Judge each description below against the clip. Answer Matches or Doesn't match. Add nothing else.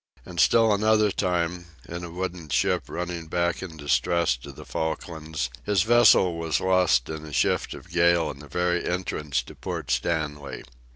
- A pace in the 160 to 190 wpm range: Matches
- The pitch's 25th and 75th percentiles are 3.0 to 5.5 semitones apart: Doesn't match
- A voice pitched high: Doesn't match